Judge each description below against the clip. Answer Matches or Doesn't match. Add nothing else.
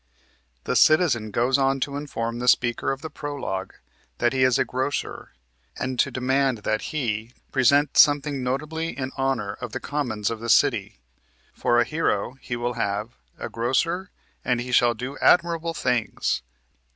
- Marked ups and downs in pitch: Doesn't match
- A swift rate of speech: Doesn't match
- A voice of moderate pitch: Doesn't match